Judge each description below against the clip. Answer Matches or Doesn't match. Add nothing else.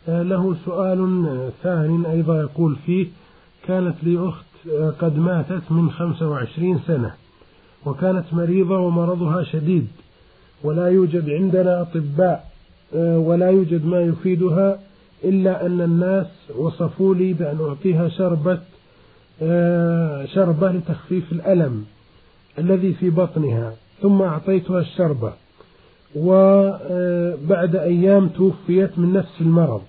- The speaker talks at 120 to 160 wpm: Doesn't match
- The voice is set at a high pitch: Doesn't match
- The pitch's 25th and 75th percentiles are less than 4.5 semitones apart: Matches